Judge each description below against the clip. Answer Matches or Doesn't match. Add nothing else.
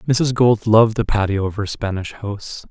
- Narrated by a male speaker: Matches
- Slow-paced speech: Doesn't match